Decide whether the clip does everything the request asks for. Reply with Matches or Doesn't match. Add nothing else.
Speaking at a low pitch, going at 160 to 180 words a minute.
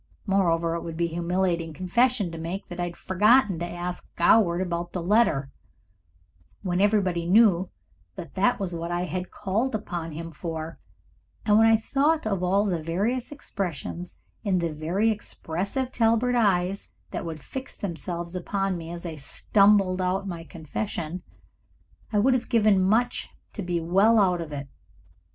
Doesn't match